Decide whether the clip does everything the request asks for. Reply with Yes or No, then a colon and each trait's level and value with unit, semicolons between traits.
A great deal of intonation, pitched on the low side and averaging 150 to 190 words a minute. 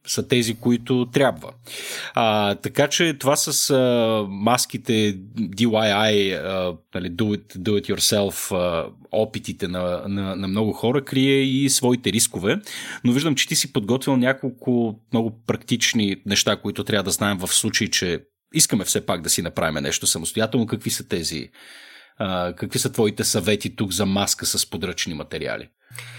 No: average, 3.7 semitones; low, 110 Hz; average, 160 wpm